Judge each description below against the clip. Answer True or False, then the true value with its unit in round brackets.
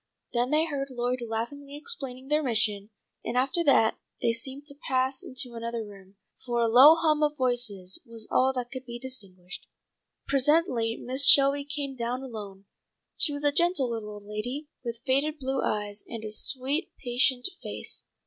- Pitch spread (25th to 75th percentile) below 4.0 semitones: True (3.5 semitones)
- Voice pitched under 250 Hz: False (255 Hz)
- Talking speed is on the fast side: False (170 wpm)